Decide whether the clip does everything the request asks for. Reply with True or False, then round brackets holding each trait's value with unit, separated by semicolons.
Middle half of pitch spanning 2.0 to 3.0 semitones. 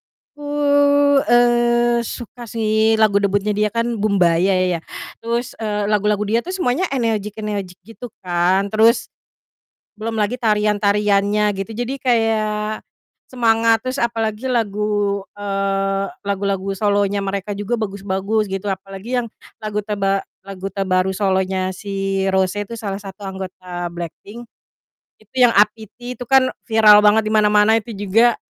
True (2.4 semitones)